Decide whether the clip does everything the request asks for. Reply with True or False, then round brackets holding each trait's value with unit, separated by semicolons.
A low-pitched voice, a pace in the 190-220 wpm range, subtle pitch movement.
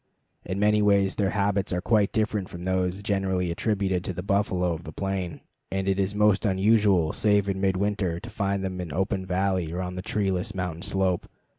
True (95 Hz; 195 wpm; 1.9 semitones)